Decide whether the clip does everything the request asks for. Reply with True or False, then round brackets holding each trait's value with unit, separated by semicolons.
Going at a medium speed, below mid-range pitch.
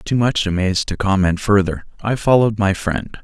True (185 wpm; 100 Hz)